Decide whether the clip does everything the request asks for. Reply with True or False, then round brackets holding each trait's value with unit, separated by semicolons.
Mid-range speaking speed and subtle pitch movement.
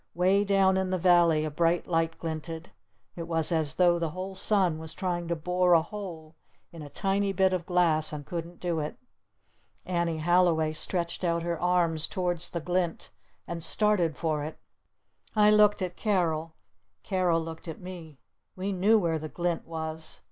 True (175 wpm; 2.3 semitones)